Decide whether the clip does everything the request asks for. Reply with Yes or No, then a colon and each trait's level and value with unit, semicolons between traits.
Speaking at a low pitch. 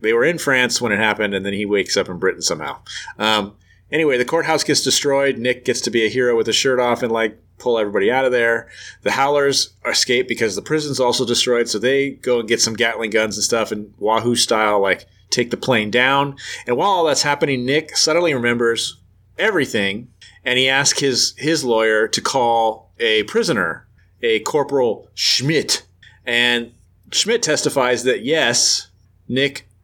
Yes: low, 125 Hz